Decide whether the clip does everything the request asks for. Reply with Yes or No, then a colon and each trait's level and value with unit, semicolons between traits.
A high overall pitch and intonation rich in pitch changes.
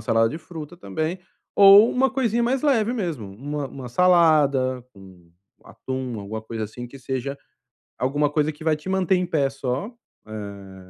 No: medium, 145 Hz; wide, 7.0 semitones